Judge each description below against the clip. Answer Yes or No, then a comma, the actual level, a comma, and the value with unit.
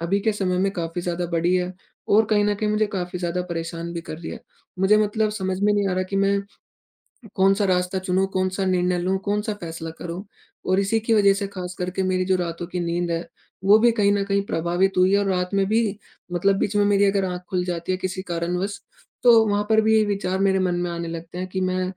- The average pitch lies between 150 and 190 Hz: Yes, medium, 185 Hz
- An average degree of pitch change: No, narrow, 2.2 semitones